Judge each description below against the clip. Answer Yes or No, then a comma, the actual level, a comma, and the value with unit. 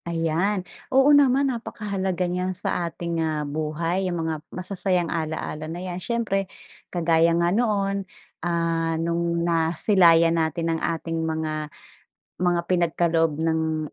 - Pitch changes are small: Yes, narrow, 2.3 semitones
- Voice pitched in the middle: Yes, medium, 170 Hz